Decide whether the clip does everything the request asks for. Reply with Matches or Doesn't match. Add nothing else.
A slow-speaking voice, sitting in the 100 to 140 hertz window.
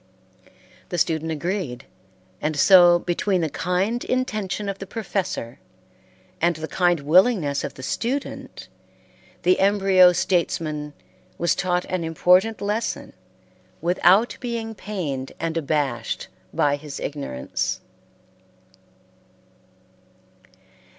Doesn't match